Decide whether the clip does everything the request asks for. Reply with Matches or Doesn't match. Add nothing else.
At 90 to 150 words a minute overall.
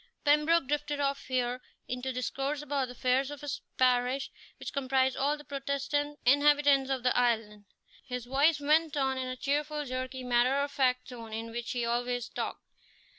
Doesn't match